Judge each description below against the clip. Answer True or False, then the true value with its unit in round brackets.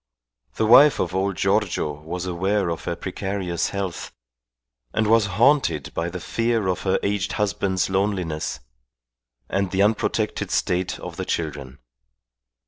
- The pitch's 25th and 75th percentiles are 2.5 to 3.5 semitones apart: True (2.9 semitones)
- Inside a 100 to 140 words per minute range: True (135 wpm)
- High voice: False (95 Hz)